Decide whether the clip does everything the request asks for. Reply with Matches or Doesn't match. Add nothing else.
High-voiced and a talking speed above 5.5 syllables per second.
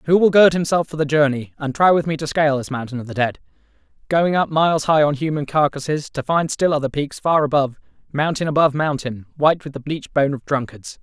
Doesn't match